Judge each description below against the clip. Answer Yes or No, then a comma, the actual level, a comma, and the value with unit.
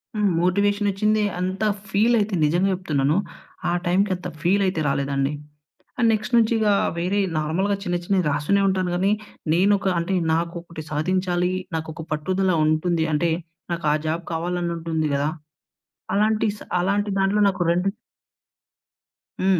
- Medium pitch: Yes, medium, 180 Hz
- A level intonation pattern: No, average, 3.3 semitones